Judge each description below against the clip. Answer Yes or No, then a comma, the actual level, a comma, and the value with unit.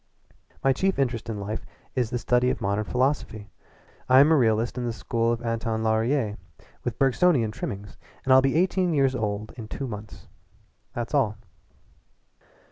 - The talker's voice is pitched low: Yes, low, 120 Hz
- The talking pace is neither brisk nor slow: Yes, average, 165 wpm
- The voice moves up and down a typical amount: Yes, average, 3.7 semitones